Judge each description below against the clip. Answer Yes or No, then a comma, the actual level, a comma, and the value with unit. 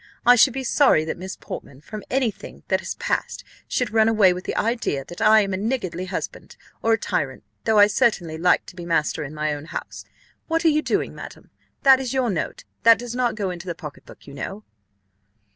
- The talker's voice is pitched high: Yes, high, 205 Hz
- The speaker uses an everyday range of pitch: No, wide, 6.0 semitones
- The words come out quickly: Yes, fast, 225 wpm